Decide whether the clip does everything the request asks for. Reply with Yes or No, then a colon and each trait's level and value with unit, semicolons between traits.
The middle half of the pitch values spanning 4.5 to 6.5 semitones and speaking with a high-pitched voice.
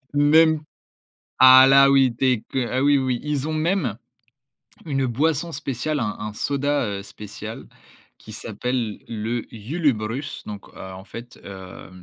No: average, 5.0 semitones; low, 130 Hz